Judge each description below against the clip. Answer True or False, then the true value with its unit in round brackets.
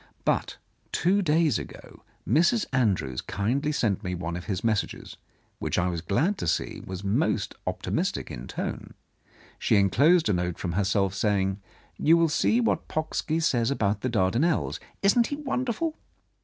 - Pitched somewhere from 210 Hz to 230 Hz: False (115 Hz)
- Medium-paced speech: True (170 wpm)